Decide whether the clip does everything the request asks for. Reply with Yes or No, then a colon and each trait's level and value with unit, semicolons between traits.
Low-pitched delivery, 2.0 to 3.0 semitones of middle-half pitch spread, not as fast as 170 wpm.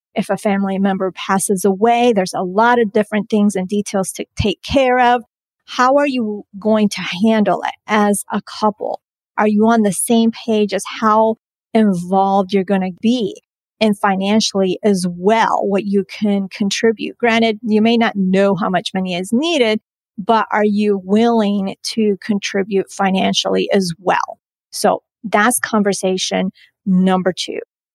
No: high, 210 Hz; narrow, 2.5 semitones; average, 155 wpm